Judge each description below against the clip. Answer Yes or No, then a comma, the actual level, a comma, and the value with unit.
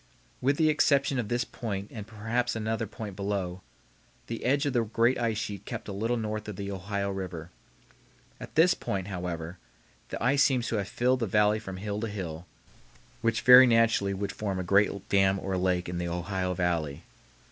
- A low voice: Yes, low, 105 Hz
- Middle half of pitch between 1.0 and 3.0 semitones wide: No, average, 3.6 semitones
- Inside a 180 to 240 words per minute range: Yes, average, 190 wpm